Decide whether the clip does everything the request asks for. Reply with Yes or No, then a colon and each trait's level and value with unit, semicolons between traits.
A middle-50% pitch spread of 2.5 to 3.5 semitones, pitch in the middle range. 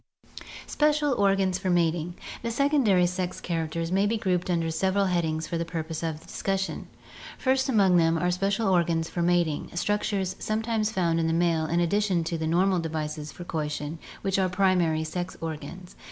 Yes: average, 3.0 semitones; medium, 175 Hz